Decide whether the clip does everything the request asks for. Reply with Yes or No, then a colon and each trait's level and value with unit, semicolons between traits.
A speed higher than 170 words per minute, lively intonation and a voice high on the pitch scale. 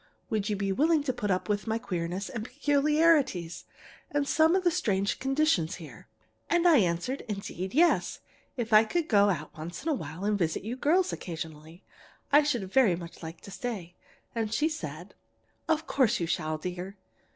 Yes: average, 185 wpm; wide, 8.6 semitones; high, 210 Hz